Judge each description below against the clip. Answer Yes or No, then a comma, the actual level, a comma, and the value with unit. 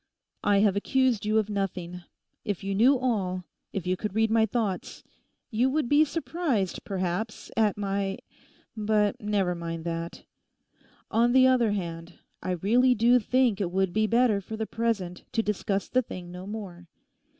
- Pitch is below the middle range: No, high, 210 Hz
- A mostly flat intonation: No, average, 3.8 semitones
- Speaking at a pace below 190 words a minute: Yes, average, 160 wpm